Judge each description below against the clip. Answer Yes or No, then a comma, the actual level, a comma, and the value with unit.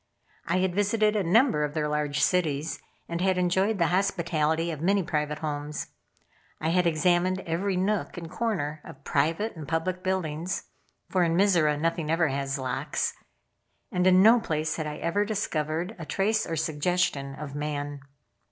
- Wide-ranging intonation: No, average, 3.8 semitones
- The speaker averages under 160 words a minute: No, average, 165 wpm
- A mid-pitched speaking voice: Yes, medium, 165 Hz